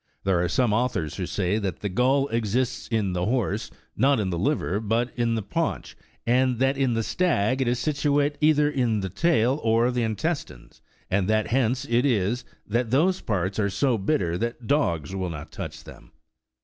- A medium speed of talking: Yes, average, 190 wpm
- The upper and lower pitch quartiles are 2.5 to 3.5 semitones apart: No, average, 4.9 semitones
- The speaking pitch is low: Yes, low, 115 Hz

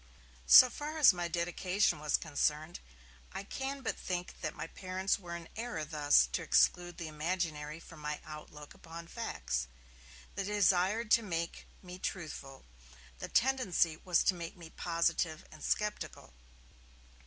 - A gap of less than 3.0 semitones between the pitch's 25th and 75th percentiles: No, average, 3.8 semitones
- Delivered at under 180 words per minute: Yes, average, 145 wpm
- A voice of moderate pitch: Yes, medium, 175 Hz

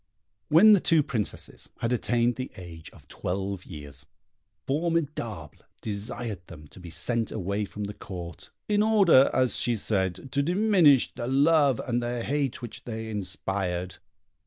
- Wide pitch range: Yes, wide, 6.7 semitones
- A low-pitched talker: Yes, low, 115 Hz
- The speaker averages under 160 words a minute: Yes, average, 150 wpm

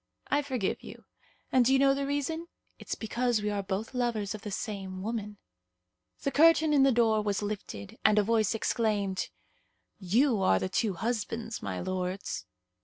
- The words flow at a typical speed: Yes, average, 175 wpm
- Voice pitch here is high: Yes, high, 220 Hz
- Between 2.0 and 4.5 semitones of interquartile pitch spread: Yes, average, 4.1 semitones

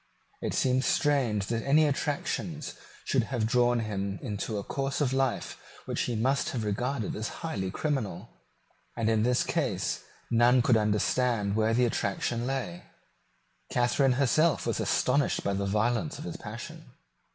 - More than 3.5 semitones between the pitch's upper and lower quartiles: Yes, average, 4.0 semitones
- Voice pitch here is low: Yes, low, 120 Hz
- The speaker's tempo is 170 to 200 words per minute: No, average, 150 wpm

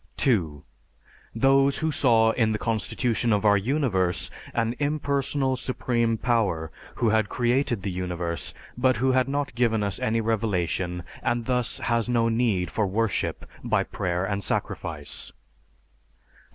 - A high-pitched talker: No, low, 115 Hz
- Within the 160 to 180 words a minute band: No, average, 140 wpm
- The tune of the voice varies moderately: Yes, average, 4.3 semitones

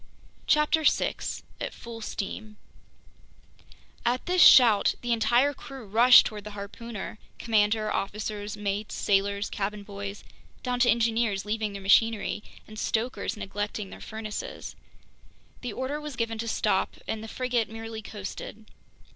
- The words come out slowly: Yes, slow, 130 wpm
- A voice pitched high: Yes, high, 220 Hz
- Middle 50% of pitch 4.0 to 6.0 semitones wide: No, narrow, 2.4 semitones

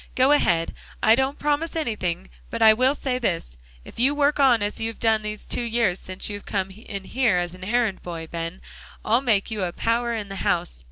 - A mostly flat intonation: No, average, 4.8 semitones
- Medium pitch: No, high, 220 Hz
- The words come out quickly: Yes, fast, 215 wpm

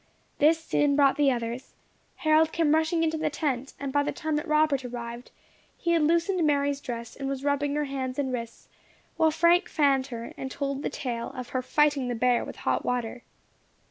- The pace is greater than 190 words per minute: Yes, average, 200 wpm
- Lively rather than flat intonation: No, average, 3.4 semitones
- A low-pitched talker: No, very high, 280 Hz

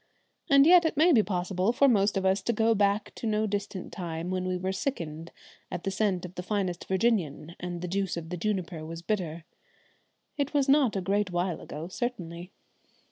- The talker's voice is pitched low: No, high, 190 Hz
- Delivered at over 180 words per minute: Yes, average, 195 wpm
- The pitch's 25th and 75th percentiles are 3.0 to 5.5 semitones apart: Yes, average, 3.7 semitones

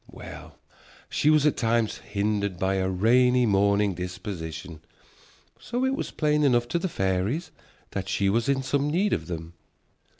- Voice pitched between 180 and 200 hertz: No, low, 105 Hz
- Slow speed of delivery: No, average, 160 wpm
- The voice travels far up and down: Yes, wide, 6.9 semitones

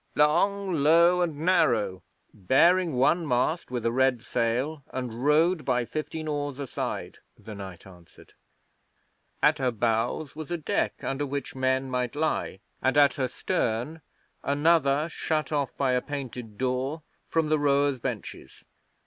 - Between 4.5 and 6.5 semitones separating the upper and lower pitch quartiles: No, average, 3.9 semitones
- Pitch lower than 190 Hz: Yes, medium, 140 Hz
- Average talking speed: Yes, average, 150 wpm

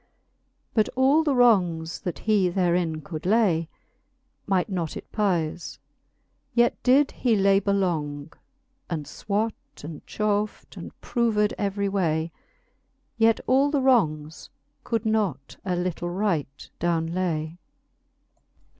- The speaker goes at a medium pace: No, slow, 120 wpm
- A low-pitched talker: No, high, 190 Hz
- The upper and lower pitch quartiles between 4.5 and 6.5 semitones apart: Yes, average, 5.0 semitones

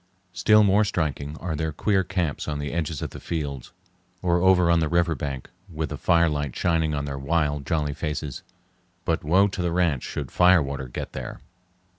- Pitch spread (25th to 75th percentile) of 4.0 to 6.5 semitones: No, average, 3.2 semitones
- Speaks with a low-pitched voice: Yes, very low, 80 Hz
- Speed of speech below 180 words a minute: No, average, 190 wpm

